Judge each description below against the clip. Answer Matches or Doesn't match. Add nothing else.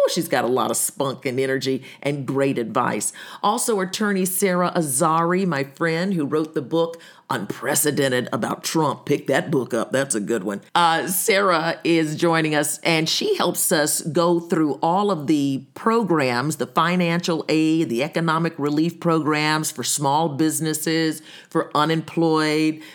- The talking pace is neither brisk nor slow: Matches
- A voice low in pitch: Doesn't match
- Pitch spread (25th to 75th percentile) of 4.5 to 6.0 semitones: Doesn't match